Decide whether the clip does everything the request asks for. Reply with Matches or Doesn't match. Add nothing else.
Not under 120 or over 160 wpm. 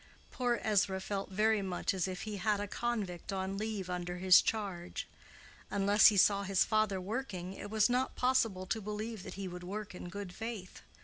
Doesn't match